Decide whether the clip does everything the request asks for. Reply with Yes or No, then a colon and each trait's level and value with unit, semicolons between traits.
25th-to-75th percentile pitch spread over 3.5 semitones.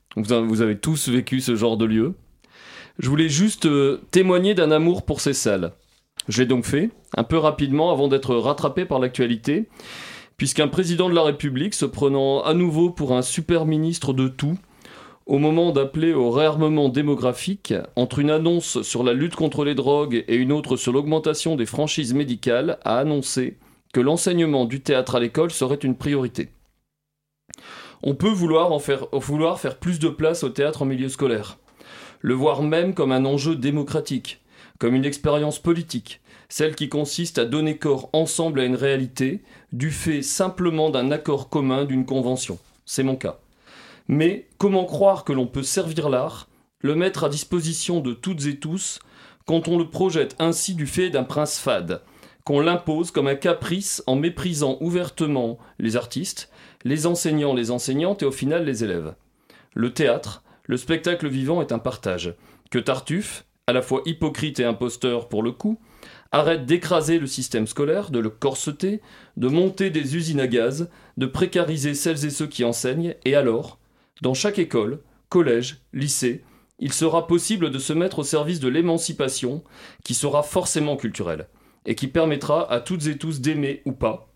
Yes: average, 4.0 semitones